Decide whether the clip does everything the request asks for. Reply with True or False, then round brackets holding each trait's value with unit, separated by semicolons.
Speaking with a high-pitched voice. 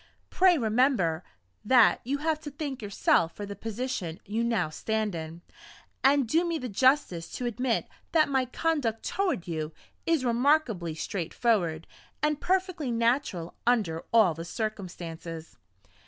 True (230 Hz)